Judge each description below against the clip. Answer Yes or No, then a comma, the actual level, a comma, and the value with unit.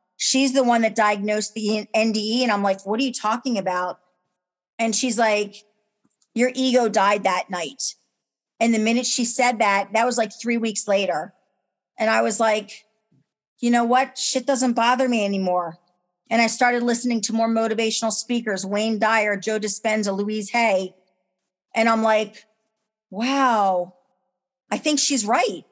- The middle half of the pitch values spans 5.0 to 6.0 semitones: No, average, 3.0 semitones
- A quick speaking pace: No, average, 160 wpm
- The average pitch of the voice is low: No, high, 220 Hz